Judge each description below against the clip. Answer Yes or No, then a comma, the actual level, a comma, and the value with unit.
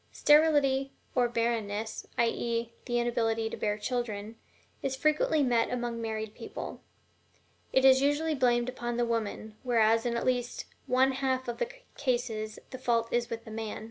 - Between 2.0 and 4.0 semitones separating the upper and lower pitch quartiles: Yes, narrow, 2.5 semitones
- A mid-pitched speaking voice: No, high, 240 Hz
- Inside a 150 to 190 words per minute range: Yes, average, 170 wpm